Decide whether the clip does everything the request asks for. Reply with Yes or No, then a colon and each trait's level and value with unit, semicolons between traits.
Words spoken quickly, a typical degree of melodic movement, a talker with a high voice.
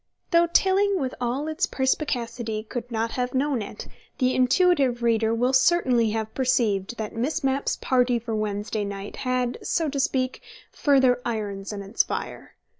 No: average, 160 wpm; average, 3.4 semitones; very high, 250 Hz